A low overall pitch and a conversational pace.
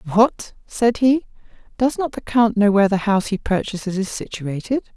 No: high, 215 Hz; average, 180 wpm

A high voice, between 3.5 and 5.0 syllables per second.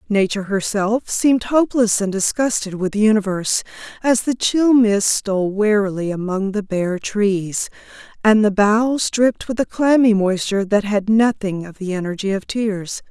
Yes: high, 210 Hz; 4.8 syllables/s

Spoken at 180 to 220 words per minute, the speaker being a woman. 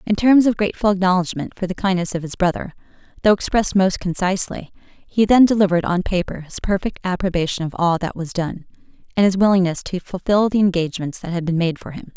Yes: average, 200 wpm; female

